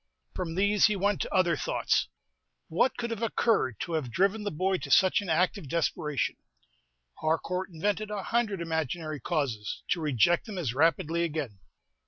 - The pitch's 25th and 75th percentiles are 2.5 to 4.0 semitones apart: No, average, 4.4 semitones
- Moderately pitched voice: Yes, medium, 170 Hz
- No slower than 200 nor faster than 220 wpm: No, average, 175 wpm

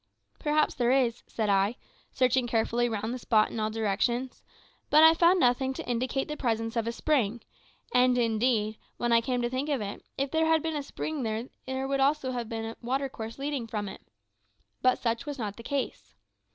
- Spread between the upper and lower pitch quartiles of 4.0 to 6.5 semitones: No, average, 3.3 semitones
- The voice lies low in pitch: No, high, 245 Hz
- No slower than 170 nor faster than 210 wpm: Yes, fast, 205 wpm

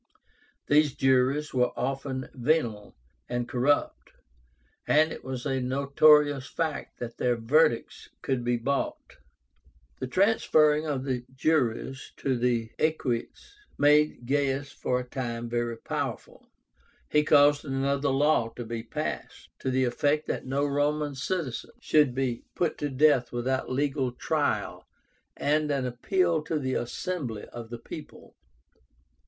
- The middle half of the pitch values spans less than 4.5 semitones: Yes, average, 3.3 semitones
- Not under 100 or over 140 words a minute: Yes, slow, 135 wpm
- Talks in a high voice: No, low, 135 Hz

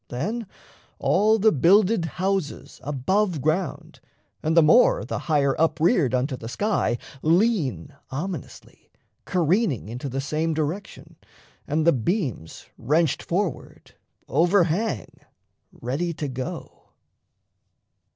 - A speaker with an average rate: No, slow, 110 wpm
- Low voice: No, medium, 160 Hz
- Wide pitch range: Yes, wide, 5.9 semitones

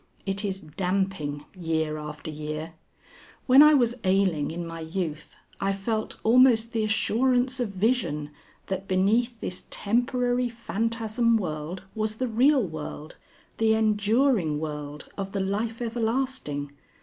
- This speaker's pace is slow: Yes, slow, 130 wpm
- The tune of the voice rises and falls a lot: Yes, wide, 6.2 semitones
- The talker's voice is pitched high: Yes, high, 200 Hz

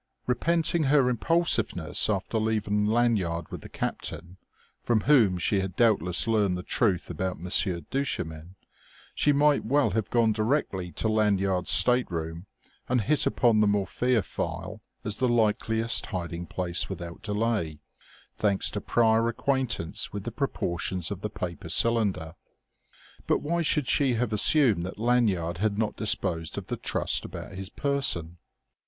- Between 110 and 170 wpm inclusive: Yes, average, 145 wpm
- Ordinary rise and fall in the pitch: Yes, average, 4.9 semitones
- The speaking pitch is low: Yes, low, 105 Hz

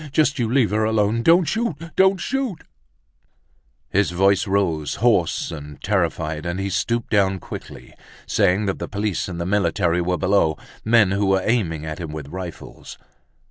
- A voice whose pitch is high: No, low, 100 Hz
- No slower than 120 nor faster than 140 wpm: No, average, 160 wpm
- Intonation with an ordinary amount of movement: Yes, average, 4.9 semitones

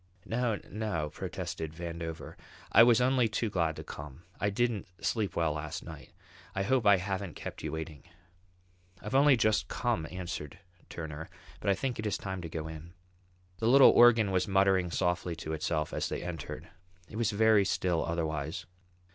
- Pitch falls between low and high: No, very low, 95 Hz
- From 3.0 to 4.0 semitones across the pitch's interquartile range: No, average, 5.3 semitones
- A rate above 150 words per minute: Yes, average, 170 wpm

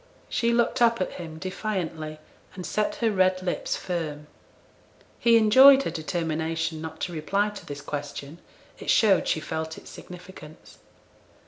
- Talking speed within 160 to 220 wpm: No, average, 145 wpm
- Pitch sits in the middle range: Yes, medium, 175 Hz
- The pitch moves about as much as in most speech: Yes, average, 4.7 semitones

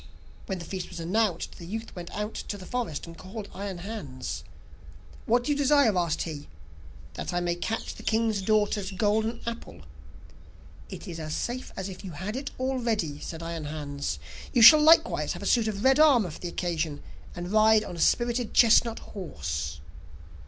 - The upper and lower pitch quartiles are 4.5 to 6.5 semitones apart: Yes, average, 5.2 semitones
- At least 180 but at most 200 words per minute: Yes, average, 185 wpm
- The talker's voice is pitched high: Yes, high, 200 Hz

